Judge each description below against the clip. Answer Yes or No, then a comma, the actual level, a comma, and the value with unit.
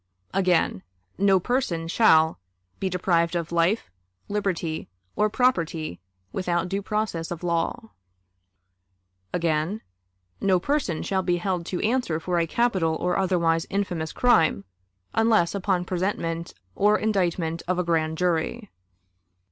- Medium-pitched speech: Yes, medium, 180 Hz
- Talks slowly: Yes, slow, 125 wpm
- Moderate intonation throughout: Yes, average, 3.3 semitones